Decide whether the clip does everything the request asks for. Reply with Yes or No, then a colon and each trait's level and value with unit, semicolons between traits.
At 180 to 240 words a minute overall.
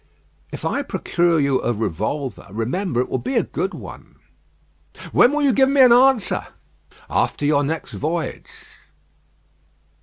No: average, 145 wpm